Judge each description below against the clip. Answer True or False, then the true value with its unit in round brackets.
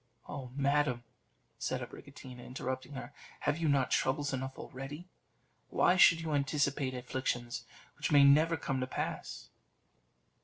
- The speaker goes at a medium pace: False (130 wpm)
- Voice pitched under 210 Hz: True (135 Hz)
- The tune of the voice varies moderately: False (2.2 semitones)